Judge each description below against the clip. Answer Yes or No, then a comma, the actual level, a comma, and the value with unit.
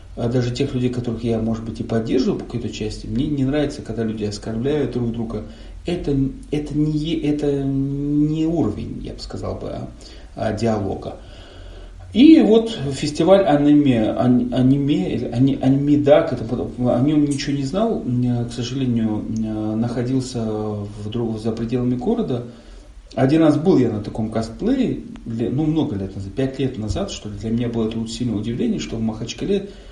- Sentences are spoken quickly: No, average, 150 wpm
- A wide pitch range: No, average, 4.3 semitones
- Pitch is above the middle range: No, low, 120 Hz